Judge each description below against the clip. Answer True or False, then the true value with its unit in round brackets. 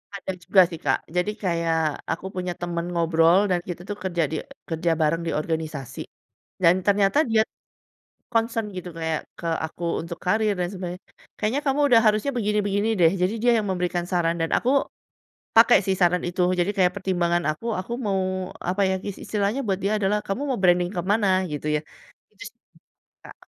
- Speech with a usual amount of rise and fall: True (3.4 semitones)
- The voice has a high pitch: False (180 Hz)